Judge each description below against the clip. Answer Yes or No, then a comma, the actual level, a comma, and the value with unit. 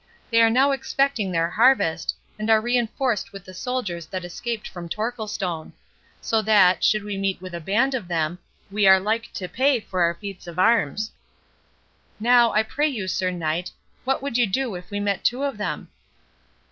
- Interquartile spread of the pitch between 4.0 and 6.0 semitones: Yes, average, 4.6 semitones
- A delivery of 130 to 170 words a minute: No, average, 185 wpm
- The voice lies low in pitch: No, high, 210 Hz